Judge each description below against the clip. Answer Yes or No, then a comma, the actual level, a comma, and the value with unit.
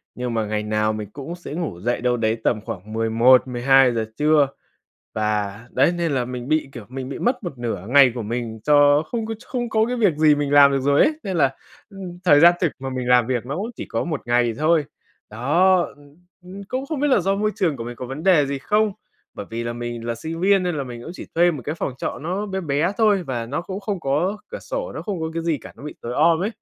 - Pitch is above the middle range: No, medium, 145 Hz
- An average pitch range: No, wide, 6.8 semitones